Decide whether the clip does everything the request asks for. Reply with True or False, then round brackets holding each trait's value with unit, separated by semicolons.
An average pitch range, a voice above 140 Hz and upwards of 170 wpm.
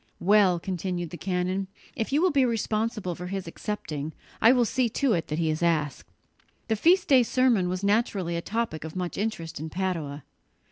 True (5.0 semitones; 190 Hz; 190 wpm)